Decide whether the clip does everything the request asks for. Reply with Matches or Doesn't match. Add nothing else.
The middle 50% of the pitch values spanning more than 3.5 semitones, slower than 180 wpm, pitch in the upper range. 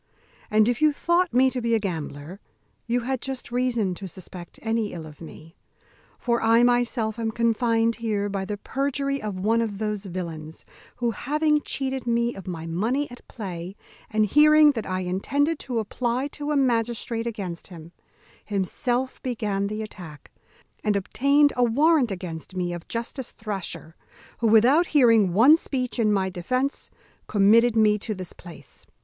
Matches